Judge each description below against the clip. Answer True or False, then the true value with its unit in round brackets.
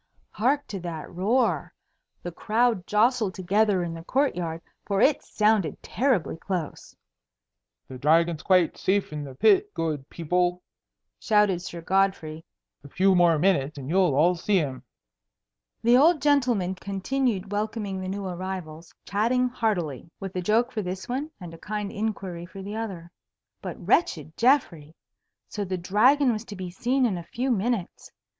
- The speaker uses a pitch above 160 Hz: True (190 Hz)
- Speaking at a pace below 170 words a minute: True (160 wpm)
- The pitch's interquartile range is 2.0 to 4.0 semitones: False (4.5 semitones)